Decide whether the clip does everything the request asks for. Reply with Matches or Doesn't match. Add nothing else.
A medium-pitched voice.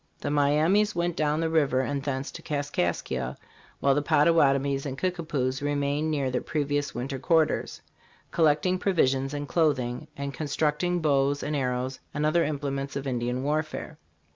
Matches